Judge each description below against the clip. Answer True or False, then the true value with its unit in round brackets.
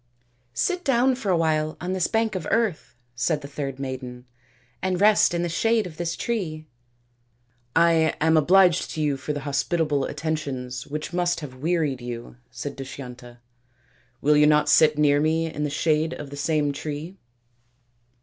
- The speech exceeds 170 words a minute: True (180 wpm)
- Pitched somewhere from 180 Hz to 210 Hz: False (150 Hz)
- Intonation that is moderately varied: True (4.0 semitones)